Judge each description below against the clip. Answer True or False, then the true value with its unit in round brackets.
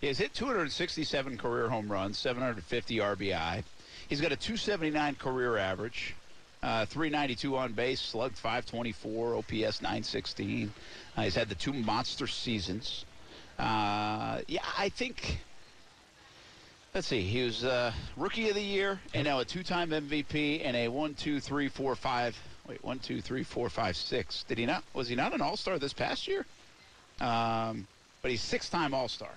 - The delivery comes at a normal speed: True (160 wpm)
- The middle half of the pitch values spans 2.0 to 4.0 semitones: False (5.2 semitones)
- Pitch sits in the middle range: False (125 Hz)